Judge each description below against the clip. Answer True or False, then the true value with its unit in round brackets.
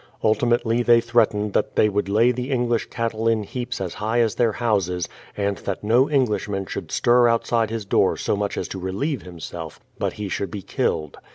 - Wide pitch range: False (3.1 semitones)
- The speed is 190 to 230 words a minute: True (195 wpm)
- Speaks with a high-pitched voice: False (110 Hz)